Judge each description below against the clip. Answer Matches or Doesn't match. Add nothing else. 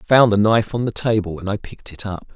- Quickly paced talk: Matches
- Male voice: Matches